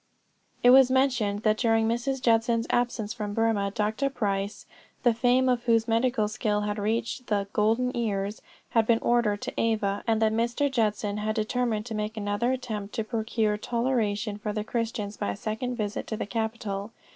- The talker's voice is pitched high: Yes, high, 220 Hz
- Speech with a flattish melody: Yes, narrow, 2.3 semitones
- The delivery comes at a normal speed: Yes, average, 180 wpm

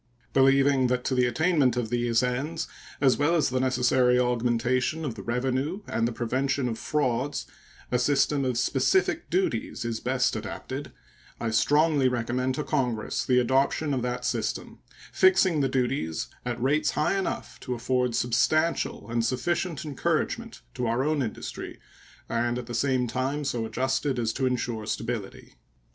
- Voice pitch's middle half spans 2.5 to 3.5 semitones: Yes, average, 2.8 semitones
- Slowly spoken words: No, average, 155 wpm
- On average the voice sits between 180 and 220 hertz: No, low, 130 Hz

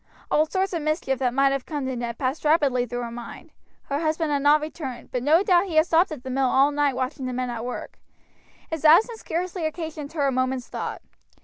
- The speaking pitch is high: Yes, very high, 290 Hz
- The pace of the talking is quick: Yes, fast, 230 wpm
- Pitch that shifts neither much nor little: Yes, average, 3.8 semitones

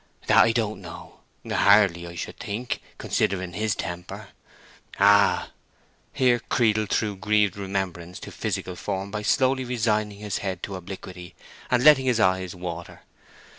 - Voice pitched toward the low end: Yes, low, 100 Hz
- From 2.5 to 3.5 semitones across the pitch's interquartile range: Yes, average, 2.9 semitones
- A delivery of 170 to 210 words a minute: No, slow, 135 wpm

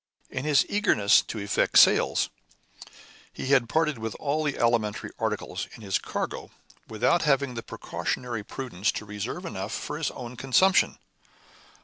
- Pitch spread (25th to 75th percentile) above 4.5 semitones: Yes, average, 5.2 semitones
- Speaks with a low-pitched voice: Yes, low, 125 Hz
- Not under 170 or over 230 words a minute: No, average, 145 wpm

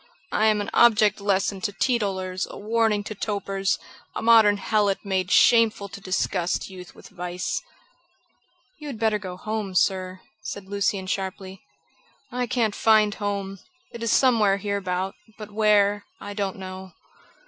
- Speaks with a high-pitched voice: Yes, high, 200 Hz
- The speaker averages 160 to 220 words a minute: No, average, 150 wpm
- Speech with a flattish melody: Yes, narrow, 2.1 semitones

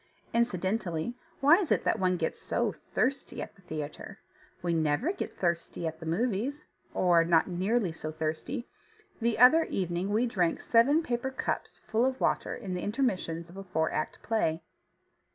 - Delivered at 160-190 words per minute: Yes, average, 170 wpm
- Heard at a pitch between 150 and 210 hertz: Yes, high, 190 Hz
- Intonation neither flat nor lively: No, wide, 6.3 semitones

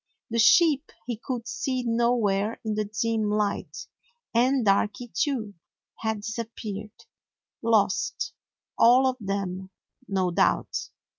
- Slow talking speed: Yes, slow, 120 wpm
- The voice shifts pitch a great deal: No, average, 2.9 semitones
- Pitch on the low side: No, high, 220 Hz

